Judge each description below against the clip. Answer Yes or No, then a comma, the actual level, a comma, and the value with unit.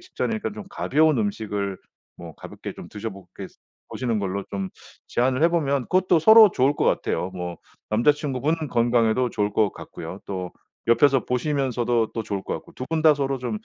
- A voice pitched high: No, low, 120 Hz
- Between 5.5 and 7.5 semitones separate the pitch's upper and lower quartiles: Yes, wide, 6.4 semitones